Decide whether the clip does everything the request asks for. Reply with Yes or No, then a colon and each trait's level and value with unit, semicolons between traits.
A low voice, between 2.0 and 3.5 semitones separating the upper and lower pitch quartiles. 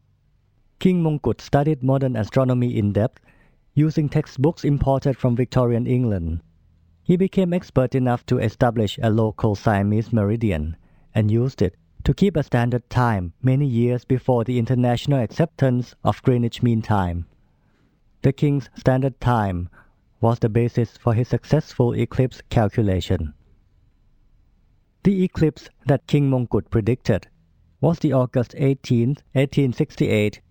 No: low, 120 Hz; average, 4.2 semitones